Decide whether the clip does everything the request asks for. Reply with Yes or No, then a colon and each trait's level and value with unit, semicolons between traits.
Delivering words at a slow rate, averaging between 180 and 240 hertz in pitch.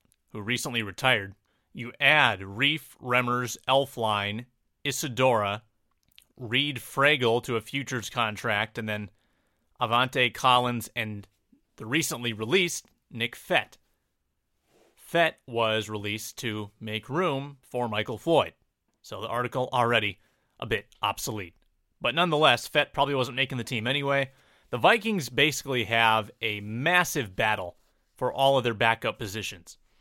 No: slow, 125 wpm; low, 120 Hz